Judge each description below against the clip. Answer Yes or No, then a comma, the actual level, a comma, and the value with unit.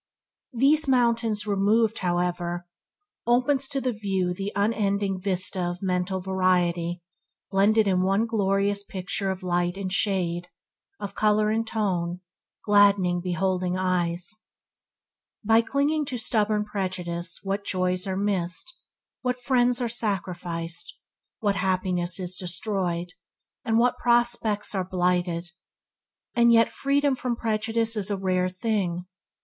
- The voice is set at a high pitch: Yes, high, 195 Hz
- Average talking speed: No, slow, 125 wpm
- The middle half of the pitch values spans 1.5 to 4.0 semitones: Yes, average, 3.6 semitones